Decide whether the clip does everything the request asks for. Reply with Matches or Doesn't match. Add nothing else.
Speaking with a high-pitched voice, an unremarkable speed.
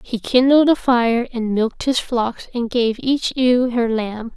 Matches